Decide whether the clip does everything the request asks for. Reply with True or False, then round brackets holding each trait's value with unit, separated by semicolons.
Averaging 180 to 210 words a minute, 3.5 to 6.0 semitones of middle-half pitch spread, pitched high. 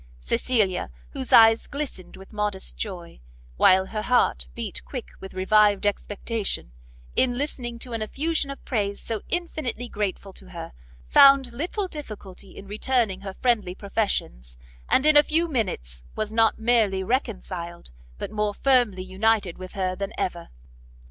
False (150 wpm; 4.6 semitones; 210 Hz)